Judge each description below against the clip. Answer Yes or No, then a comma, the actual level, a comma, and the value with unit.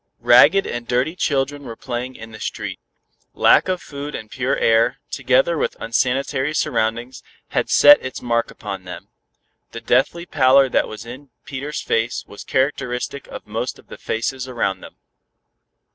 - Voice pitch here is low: Yes, low, 130 Hz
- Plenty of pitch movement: No, average, 3.1 semitones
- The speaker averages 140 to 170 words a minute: Yes, average, 160 wpm